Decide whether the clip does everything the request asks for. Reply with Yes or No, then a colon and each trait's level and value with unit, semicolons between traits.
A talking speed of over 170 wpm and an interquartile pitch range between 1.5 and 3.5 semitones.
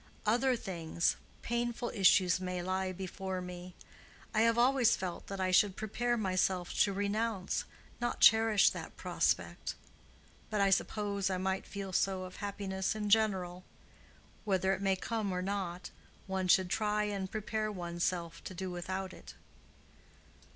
No: average, 145 wpm; narrow, 2.5 semitones